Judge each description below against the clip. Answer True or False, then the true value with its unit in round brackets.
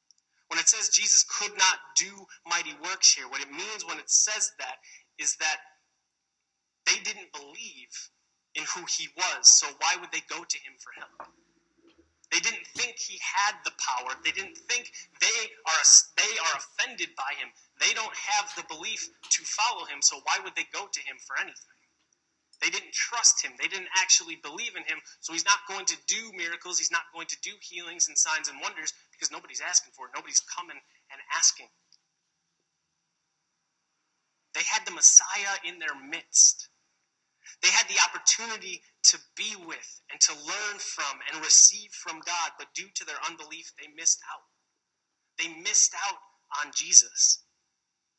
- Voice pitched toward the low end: False (175 Hz)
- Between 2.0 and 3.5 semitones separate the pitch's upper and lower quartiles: False (4.5 semitones)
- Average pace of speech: True (175 wpm)